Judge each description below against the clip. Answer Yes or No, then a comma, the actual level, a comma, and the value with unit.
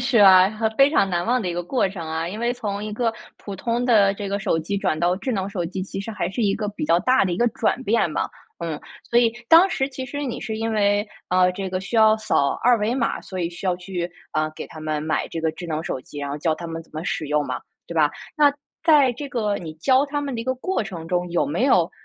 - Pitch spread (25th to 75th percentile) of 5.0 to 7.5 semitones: Yes, wide, 5.5 semitones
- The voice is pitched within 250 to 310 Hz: No, high, 195 Hz